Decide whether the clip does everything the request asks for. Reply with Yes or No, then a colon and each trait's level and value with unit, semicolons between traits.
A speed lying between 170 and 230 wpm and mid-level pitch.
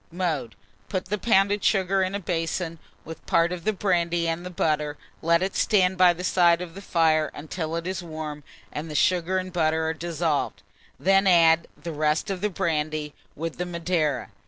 Yes: average, 190 wpm; medium, 170 Hz